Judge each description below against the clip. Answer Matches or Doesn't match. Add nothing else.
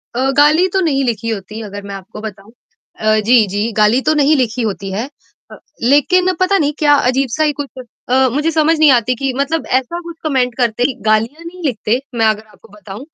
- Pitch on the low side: Doesn't match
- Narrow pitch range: Doesn't match